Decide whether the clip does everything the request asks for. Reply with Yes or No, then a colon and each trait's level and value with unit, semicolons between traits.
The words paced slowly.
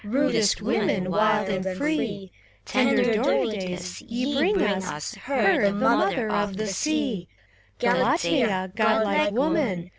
Yes: slow, 120 wpm